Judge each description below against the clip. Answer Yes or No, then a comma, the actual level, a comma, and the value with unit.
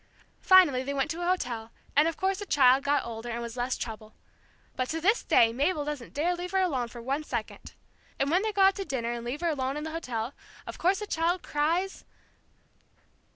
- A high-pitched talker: Yes, very high, 290 Hz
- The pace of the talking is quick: Yes, fast, 220 wpm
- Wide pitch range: Yes, wide, 6.2 semitones